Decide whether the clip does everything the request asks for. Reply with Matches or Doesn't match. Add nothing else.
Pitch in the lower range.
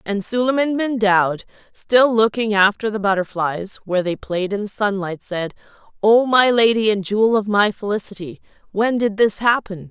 Doesn't match